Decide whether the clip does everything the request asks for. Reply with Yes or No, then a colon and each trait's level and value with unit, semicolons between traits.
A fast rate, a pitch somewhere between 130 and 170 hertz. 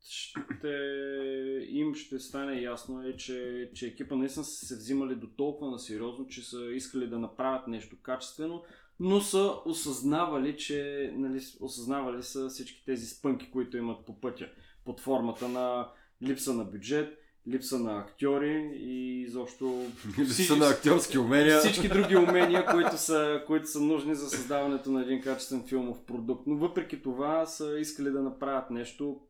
No: average, 155 wpm; low, 135 Hz